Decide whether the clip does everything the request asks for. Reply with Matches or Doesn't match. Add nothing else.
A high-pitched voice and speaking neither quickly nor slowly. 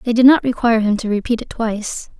Doesn't match